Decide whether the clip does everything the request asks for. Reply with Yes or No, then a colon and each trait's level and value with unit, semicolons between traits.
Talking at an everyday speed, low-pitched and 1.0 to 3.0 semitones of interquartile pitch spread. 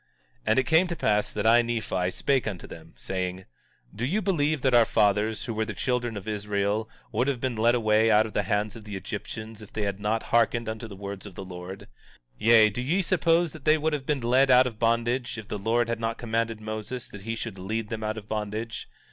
No: fast, 240 wpm; low, 110 Hz; average, 2.7 semitones